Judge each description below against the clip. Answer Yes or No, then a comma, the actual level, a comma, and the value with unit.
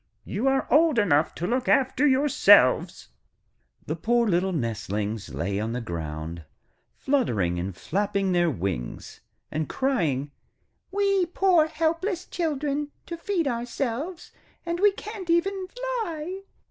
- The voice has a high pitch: Yes, very high, 250 Hz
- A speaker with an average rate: No, slow, 125 wpm